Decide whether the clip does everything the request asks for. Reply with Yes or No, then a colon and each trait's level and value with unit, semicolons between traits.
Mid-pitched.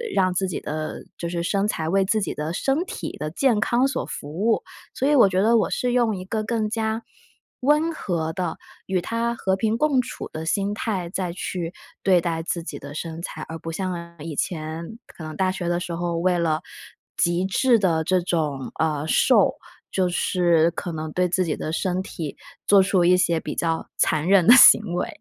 Yes: medium, 180 Hz